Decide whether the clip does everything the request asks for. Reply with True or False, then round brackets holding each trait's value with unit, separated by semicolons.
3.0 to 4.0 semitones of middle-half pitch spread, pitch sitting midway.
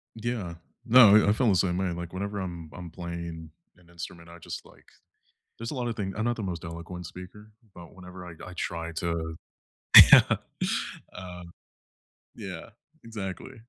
False (3.3 semitones; 90 Hz)